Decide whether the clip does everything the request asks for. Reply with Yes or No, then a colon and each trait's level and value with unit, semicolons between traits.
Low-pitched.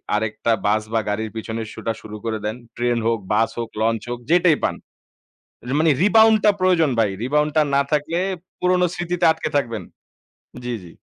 Yes: low, 120 Hz